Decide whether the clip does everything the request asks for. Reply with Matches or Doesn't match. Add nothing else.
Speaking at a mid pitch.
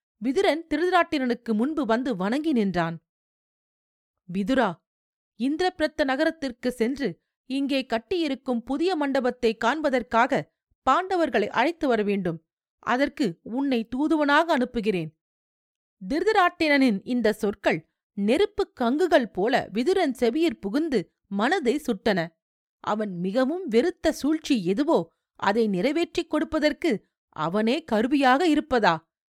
Doesn't match